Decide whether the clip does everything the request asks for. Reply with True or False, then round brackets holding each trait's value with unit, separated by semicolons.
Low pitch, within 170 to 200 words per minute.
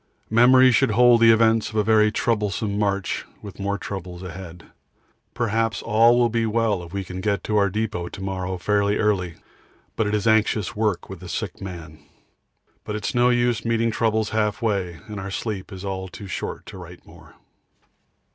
True (105 Hz; 185 wpm)